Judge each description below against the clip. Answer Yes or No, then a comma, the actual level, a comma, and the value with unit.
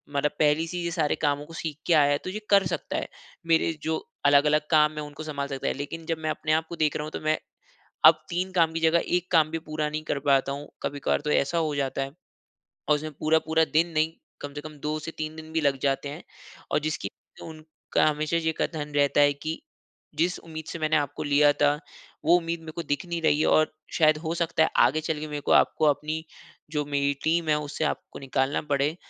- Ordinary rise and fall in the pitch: No, narrow, 1.7 semitones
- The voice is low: No, medium, 155 Hz